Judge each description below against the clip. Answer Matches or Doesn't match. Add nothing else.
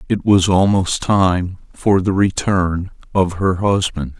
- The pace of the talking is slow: Doesn't match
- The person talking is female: Doesn't match